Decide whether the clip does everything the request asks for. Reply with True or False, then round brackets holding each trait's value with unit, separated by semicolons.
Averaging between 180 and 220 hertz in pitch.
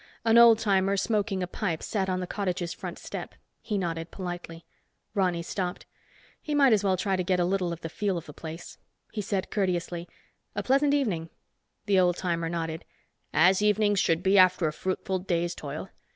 True (185 Hz)